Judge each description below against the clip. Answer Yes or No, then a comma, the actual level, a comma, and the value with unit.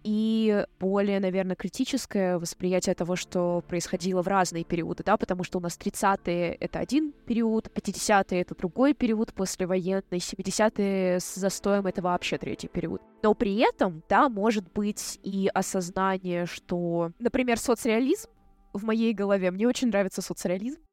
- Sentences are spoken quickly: No, average, 145 wpm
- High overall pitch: Yes, high, 195 Hz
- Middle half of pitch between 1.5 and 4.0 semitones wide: Yes, average, 3.4 semitones